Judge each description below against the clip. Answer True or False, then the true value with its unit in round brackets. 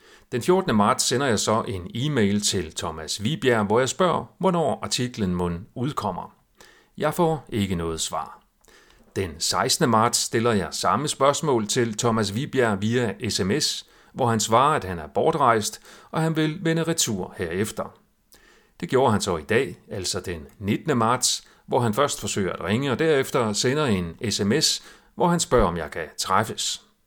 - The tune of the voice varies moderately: False (6.7 semitones)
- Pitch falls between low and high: False (115 Hz)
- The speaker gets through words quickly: False (170 wpm)